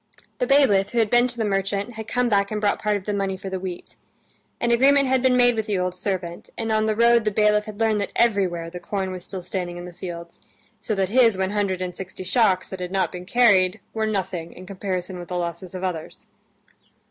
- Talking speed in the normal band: No, fast, 240 wpm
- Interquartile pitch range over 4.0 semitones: No, average, 3.2 semitones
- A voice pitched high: Yes, high, 200 Hz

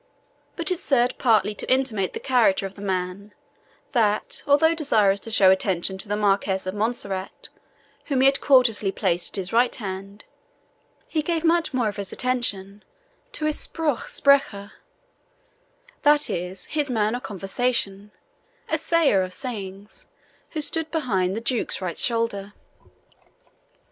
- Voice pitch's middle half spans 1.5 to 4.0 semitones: No, average, 5.3 semitones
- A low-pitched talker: No, high, 215 Hz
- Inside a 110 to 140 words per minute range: No, average, 150 wpm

